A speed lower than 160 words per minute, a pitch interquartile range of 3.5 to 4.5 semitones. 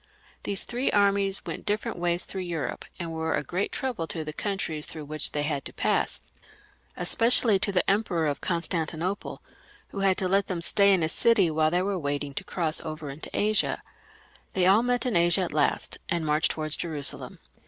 No: average, 195 wpm; average, 4.1 semitones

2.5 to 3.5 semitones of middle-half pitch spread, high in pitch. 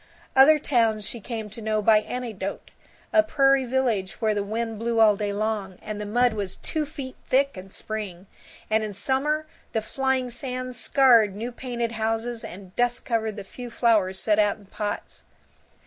Yes: average, 3.2 semitones; high, 225 Hz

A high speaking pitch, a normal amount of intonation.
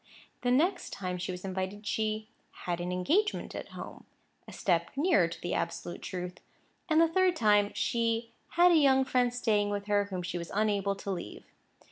No: high, 205 Hz; wide, 5.7 semitones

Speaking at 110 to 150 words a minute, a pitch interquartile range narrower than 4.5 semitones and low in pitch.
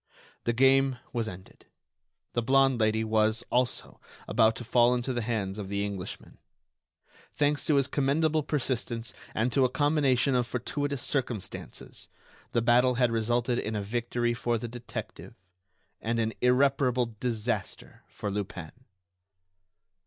Yes: average, 140 wpm; average, 2.9 semitones; low, 120 Hz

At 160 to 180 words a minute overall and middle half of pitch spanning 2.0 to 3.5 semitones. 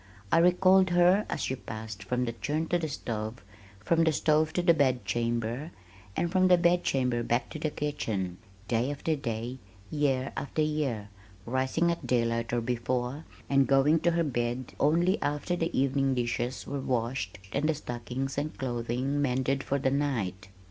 No: average, 170 wpm; average, 4.5 semitones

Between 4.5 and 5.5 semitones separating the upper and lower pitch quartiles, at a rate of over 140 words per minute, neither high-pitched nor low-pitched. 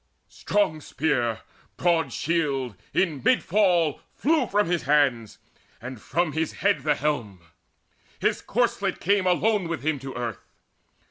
No: average, 5.1 semitones; slow, 135 wpm; medium, 155 Hz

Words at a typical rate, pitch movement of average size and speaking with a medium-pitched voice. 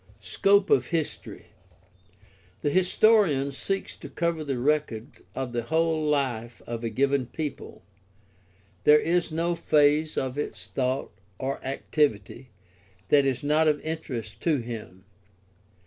No: slow, 130 wpm; average, 4.1 semitones; medium, 145 Hz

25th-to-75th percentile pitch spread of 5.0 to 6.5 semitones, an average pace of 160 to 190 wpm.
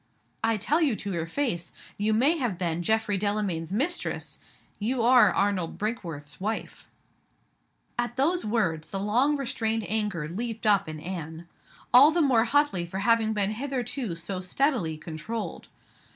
No: wide, 5.4 semitones; average, 150 wpm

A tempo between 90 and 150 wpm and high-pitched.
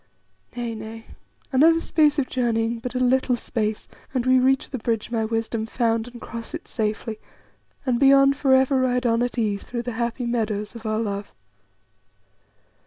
No: average, 175 wpm; high, 235 Hz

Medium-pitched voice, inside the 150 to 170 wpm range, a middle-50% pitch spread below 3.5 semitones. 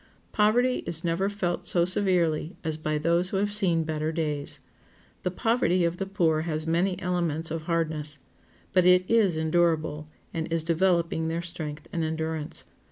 Yes: medium, 170 Hz; average, 165 wpm; narrow, 2.4 semitones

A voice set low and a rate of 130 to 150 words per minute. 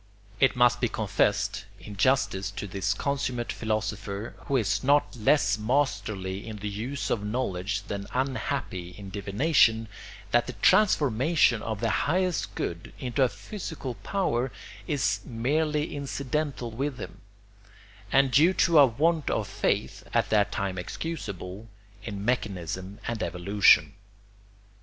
Yes: low, 115 Hz; slow, 135 wpm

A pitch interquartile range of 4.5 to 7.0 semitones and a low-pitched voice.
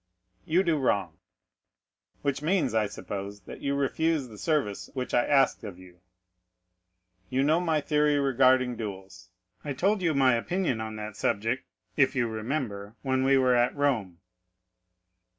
Yes: average, 5.1 semitones; low, 130 Hz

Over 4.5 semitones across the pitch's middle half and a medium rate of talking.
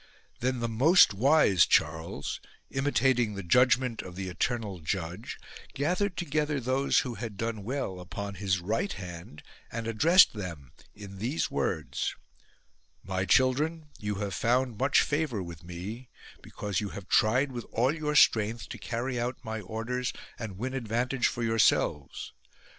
Yes: average, 5.0 semitones; average, 150 wpm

